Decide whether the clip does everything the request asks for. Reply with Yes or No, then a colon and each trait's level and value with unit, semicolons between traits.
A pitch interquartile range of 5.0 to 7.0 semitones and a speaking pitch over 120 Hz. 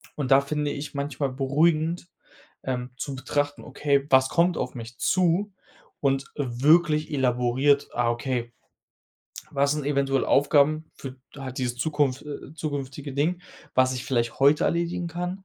No: narrow, 2.6 semitones; medium, 140 Hz